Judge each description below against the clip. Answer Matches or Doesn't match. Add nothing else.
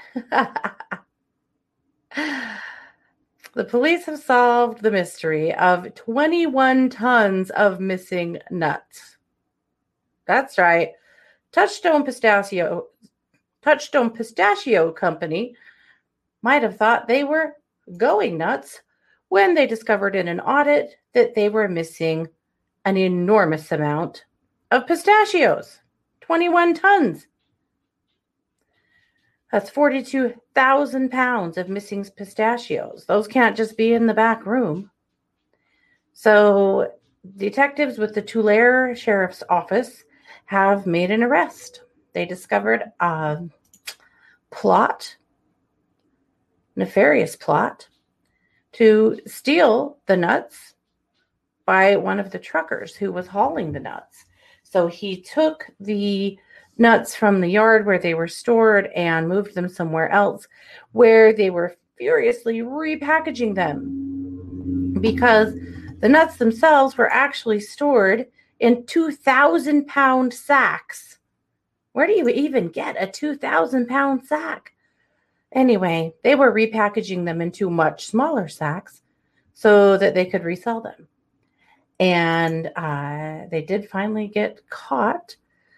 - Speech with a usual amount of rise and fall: Doesn't match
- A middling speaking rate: Doesn't match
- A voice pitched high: Matches